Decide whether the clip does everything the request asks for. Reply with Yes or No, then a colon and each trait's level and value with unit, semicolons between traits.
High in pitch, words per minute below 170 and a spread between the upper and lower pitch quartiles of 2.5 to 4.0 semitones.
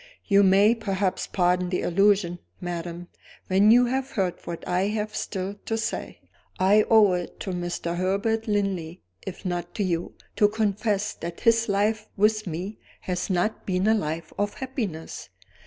Yes: high, 195 Hz; average, 160 wpm; average, 3.2 semitones